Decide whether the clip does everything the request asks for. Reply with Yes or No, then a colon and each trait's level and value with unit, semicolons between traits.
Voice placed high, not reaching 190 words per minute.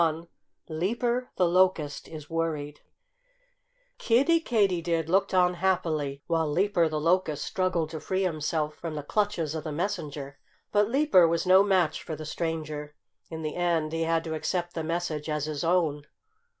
No: medium, 165 Hz; average, 165 wpm